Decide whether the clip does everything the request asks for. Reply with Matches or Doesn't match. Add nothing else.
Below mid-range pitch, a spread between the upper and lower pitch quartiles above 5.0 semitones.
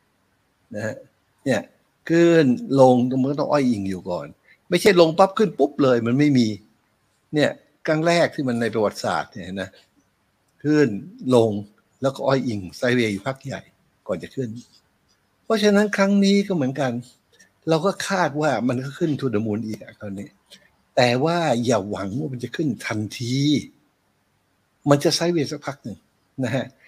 Matches